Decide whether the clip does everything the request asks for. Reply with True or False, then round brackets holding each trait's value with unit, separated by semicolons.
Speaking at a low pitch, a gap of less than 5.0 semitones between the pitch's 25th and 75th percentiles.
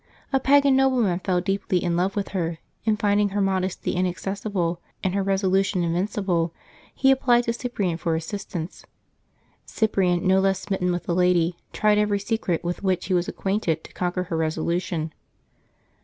False (190 Hz; 2.7 semitones)